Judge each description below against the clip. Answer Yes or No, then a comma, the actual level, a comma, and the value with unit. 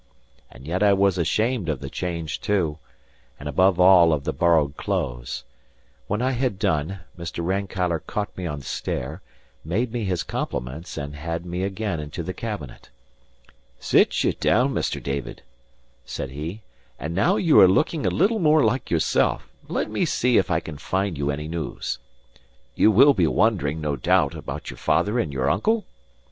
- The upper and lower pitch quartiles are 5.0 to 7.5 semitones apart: Yes, wide, 5.5 semitones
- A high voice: No, very low, 90 Hz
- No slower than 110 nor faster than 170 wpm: No, average, 180 wpm